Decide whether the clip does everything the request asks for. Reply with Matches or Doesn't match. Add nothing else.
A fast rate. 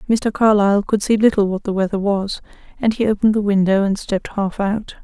Matches